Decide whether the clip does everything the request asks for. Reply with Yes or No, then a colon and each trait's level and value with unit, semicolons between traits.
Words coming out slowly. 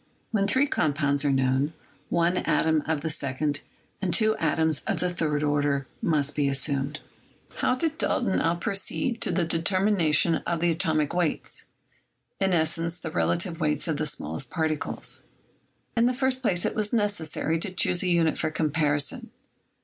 No: average, 165 wpm